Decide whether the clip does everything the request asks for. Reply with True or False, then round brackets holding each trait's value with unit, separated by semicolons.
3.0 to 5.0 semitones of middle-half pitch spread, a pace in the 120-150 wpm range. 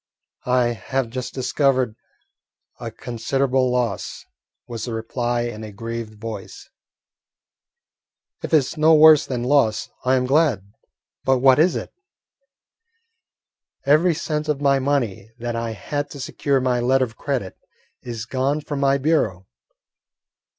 True (3.4 semitones; 135 wpm)